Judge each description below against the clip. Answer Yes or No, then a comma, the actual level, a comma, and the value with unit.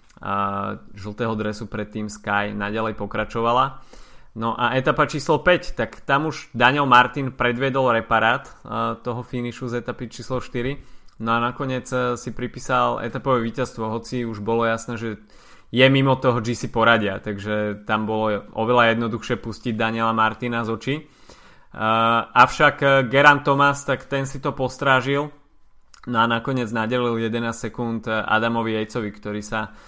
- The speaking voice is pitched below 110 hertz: No, low, 120 Hz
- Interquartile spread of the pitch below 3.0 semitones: Yes, narrow, 2.6 semitones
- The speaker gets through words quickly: No, average, 145 wpm